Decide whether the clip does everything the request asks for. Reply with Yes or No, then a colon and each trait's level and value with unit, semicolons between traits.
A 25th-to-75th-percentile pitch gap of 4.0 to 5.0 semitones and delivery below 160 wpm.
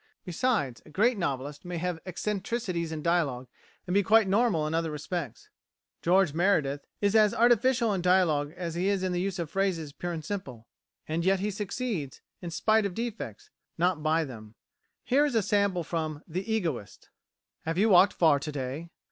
No: average, 4.6 semitones; average, 180 wpm